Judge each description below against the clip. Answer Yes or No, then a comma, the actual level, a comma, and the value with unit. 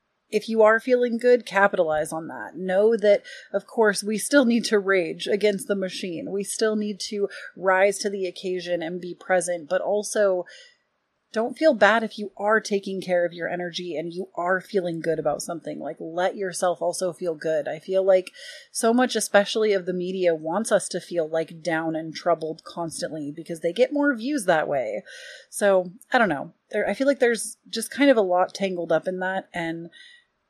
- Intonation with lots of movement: No, average, 3.8 semitones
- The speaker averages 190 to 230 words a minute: Yes, average, 200 wpm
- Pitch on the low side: No, high, 195 Hz